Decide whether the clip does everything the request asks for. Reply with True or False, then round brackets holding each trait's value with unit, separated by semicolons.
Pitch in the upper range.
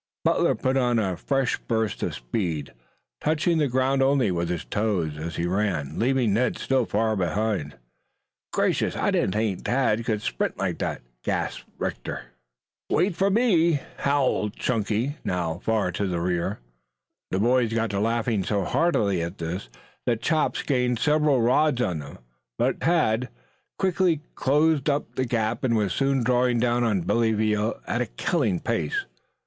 False (115 Hz)